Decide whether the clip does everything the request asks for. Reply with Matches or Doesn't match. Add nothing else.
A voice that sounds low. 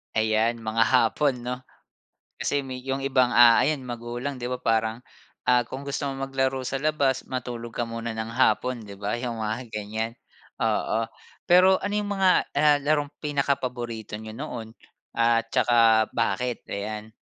Matches